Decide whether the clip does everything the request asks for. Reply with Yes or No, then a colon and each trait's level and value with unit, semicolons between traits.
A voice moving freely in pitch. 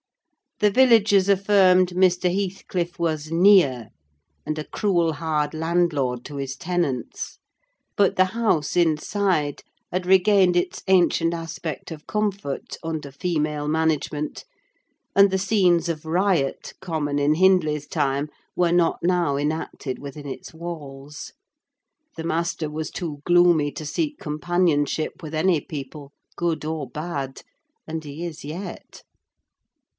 No: average, 3.4 semitones